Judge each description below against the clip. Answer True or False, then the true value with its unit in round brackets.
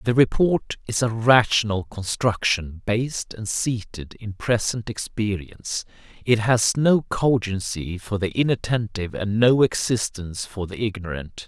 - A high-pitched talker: False (110 Hz)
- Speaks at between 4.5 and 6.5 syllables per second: False (4.3 syllables/s)